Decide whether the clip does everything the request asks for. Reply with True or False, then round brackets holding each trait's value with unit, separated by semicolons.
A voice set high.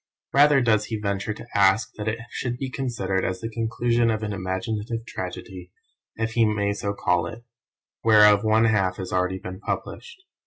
False (110 Hz)